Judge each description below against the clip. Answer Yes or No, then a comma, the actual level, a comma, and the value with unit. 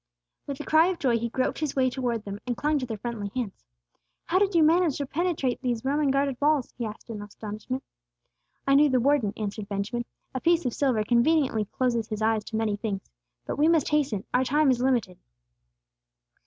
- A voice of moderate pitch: No, very high, 255 Hz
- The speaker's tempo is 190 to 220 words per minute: Yes, fast, 205 wpm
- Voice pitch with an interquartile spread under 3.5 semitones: No, average, 4.7 semitones